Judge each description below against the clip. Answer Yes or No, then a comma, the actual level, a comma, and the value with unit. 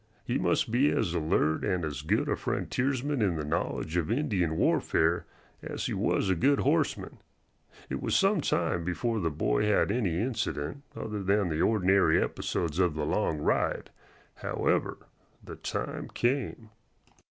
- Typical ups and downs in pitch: No, wide, 6.9 semitones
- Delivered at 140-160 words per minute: Yes, average, 155 wpm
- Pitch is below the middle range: Yes, very low, 95 Hz